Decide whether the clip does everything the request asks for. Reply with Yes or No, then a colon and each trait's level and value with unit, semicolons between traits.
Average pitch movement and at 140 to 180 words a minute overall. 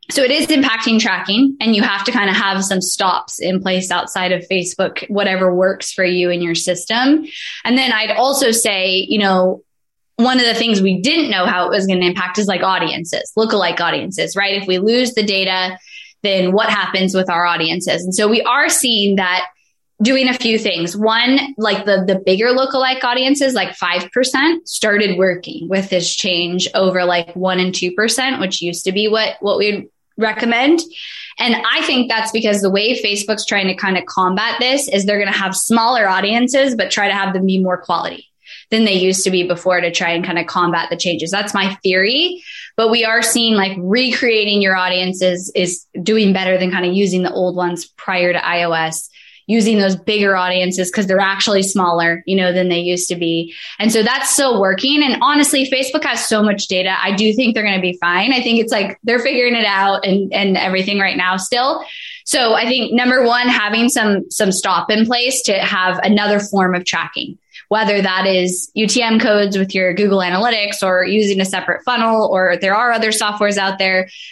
No: average, 3.9 semitones; fast, 205 wpm